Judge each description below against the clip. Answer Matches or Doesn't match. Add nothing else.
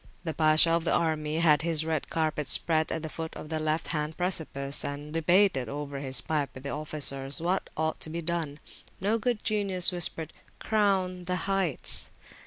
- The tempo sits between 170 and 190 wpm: Matches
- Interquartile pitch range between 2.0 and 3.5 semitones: Matches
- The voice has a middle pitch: Matches